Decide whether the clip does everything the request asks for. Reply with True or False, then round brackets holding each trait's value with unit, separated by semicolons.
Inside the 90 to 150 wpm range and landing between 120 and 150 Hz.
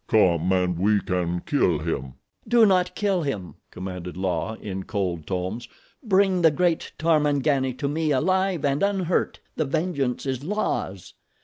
True (145 wpm; 135 Hz)